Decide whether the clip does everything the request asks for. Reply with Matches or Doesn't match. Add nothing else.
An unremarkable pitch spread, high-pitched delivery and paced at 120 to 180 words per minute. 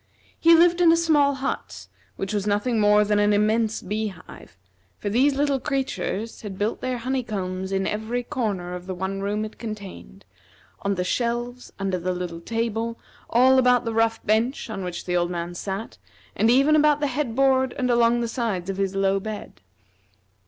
Doesn't match